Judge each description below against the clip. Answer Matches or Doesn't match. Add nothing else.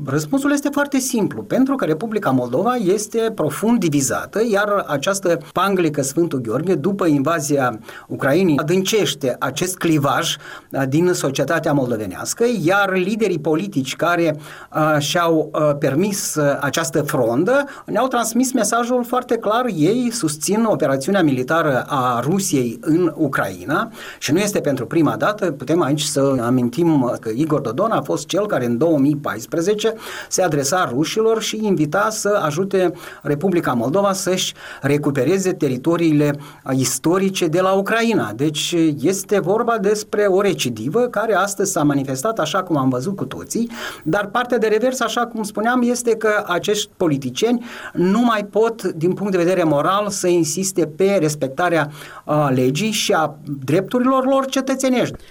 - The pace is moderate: Matches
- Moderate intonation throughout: Doesn't match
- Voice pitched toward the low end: Doesn't match